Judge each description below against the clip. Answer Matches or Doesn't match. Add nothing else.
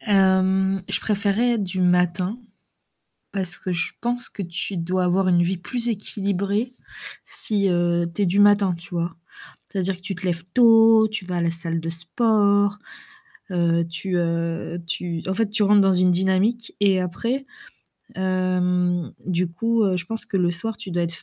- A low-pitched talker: Doesn't match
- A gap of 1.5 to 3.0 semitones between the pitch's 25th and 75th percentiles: Matches